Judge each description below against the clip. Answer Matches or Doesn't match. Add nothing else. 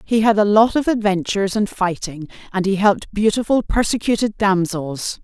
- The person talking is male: Doesn't match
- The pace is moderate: Matches